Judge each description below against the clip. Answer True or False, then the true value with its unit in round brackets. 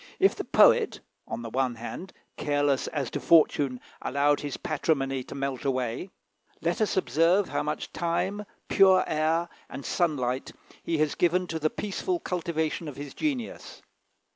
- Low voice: False (155 Hz)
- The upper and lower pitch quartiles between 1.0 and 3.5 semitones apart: False (4.2 semitones)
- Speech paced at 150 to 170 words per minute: True (155 wpm)